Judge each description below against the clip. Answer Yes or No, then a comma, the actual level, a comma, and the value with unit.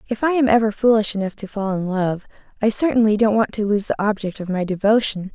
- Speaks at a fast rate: Yes, fast, 235 wpm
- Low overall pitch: No, high, 210 Hz